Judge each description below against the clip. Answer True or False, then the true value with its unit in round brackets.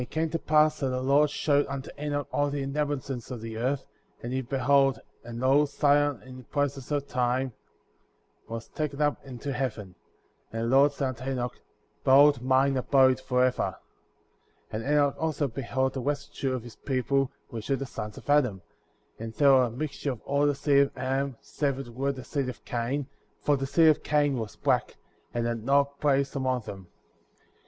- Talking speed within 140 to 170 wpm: False (195 wpm)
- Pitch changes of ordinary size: False (2.2 semitones)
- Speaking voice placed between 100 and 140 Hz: True (135 Hz)